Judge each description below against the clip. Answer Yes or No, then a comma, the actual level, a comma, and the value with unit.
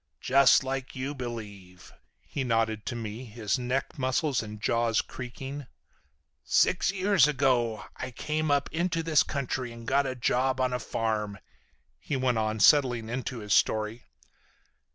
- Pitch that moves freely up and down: No, average, 3.4 semitones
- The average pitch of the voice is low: Yes, low, 125 Hz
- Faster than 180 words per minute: No, average, 150 wpm